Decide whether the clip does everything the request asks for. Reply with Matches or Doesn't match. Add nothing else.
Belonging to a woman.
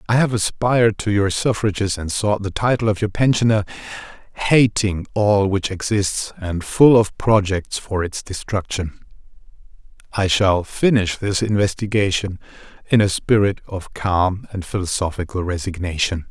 Doesn't match